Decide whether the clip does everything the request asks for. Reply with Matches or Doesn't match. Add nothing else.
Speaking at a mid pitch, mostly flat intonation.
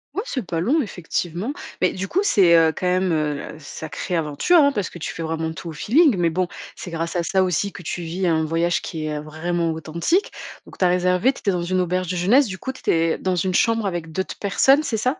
Doesn't match